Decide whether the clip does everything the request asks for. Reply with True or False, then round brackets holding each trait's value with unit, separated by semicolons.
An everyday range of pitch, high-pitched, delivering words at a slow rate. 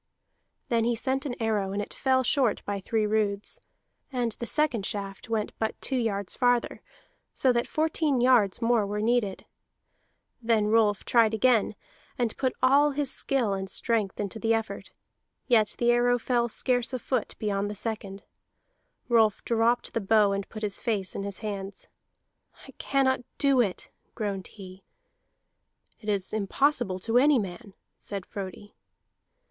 False (3.4 semitones; 225 Hz; 155 wpm)